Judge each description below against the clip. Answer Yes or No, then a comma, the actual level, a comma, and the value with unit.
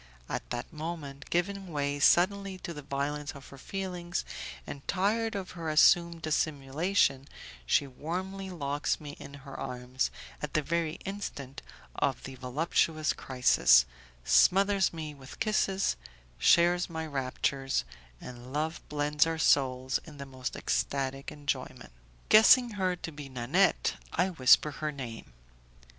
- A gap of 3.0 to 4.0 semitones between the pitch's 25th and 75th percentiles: No, average, 4.4 semitones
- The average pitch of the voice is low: No, medium, 150 Hz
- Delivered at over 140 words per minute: No, slow, 135 wpm